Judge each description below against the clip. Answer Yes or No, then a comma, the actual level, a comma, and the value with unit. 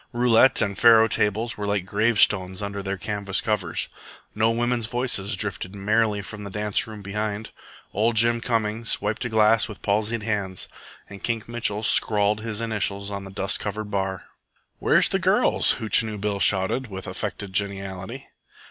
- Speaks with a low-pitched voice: Yes, low, 105 Hz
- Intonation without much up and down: Yes, narrow, 2.1 semitones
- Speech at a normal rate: Yes, average, 160 wpm